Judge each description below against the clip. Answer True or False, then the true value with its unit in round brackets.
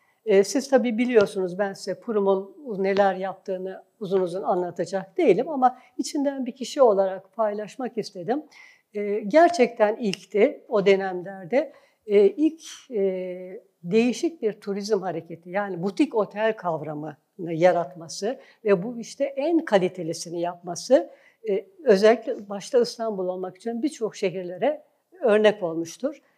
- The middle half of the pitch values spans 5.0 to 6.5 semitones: True (5.6 semitones)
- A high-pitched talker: True (210 Hz)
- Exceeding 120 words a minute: False (110 wpm)